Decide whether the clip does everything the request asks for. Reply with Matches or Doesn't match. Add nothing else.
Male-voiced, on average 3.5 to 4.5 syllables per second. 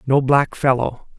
Matches